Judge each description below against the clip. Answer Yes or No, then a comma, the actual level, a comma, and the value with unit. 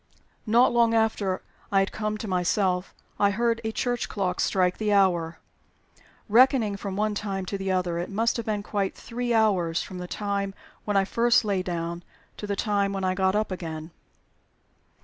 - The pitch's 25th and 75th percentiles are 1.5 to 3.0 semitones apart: Yes, average, 2.7 semitones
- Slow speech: No, average, 185 wpm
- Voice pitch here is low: No, high, 200 Hz